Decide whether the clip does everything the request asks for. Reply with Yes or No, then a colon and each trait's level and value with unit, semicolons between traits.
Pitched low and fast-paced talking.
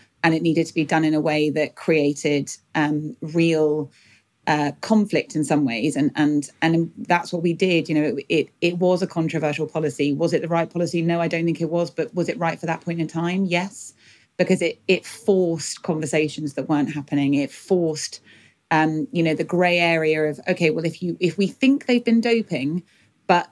No: medium, 165 Hz; fast, 210 wpm